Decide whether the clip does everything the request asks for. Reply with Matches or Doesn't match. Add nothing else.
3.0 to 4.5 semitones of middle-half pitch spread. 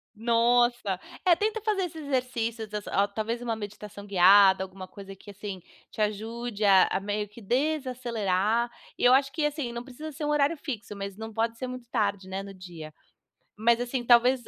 Matches